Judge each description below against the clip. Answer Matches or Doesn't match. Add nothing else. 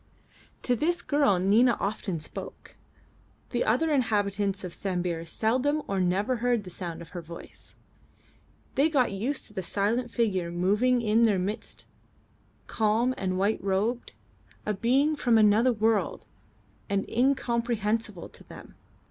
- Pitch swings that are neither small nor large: Matches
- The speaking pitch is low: Doesn't match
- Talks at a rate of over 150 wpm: Doesn't match